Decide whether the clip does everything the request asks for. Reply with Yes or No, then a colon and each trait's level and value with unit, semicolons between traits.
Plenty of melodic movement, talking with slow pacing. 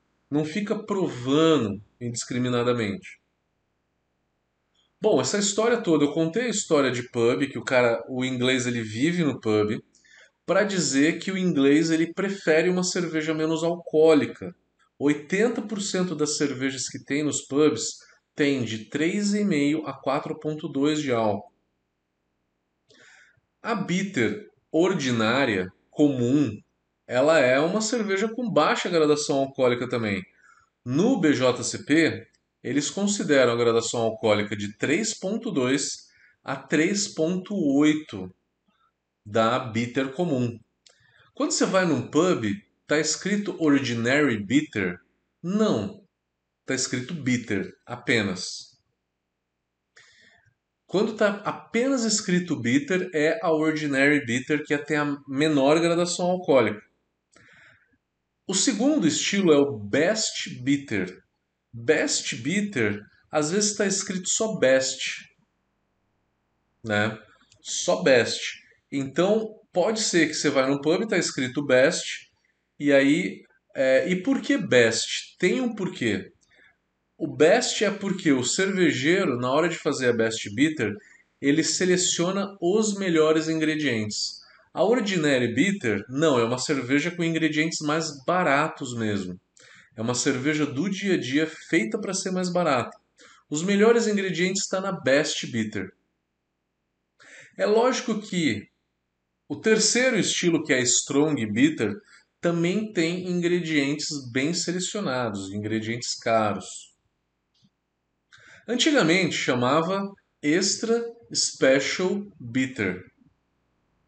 Yes: wide, 7.0 semitones; slow, 115 wpm